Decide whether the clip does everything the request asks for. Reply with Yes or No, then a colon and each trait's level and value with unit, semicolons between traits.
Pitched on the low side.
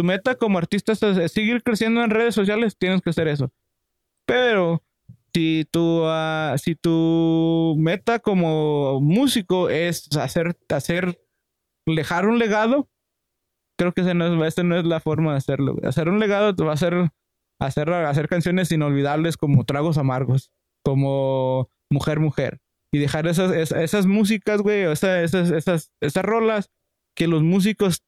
No: medium, 165 Hz